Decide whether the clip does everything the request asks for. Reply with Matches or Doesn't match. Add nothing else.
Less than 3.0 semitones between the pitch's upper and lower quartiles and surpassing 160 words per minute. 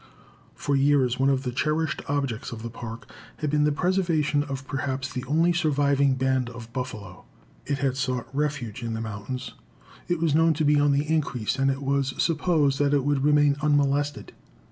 Matches